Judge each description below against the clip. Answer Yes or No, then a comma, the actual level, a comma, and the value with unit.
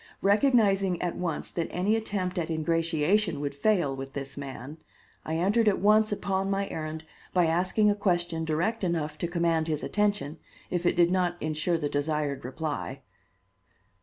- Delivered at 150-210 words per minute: Yes, average, 165 wpm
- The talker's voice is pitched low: No, medium, 170 Hz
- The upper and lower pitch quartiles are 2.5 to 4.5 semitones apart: Yes, average, 4.0 semitones